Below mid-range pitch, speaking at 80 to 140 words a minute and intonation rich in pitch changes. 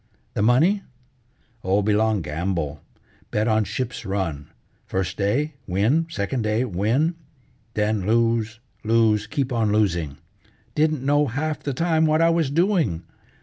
Yes: low, 110 Hz; slow, 135 wpm; wide, 6.6 semitones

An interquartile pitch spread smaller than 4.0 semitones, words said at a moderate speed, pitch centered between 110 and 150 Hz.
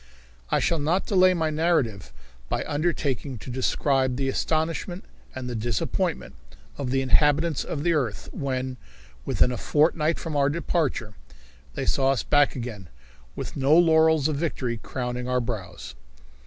No: average, 4.3 semitones; average, 150 wpm; medium, 140 Hz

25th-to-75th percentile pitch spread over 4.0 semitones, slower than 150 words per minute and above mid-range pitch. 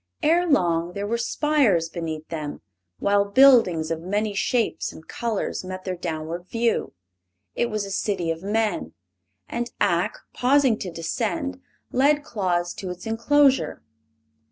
Yes: wide, 5.6 semitones; average, 140 wpm; high, 200 Hz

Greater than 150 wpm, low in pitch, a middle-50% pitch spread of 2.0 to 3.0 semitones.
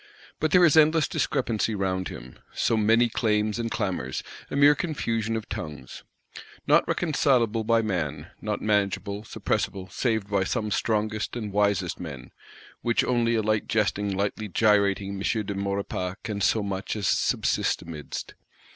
No: average, 145 wpm; low, 105 Hz; average, 2.7 semitones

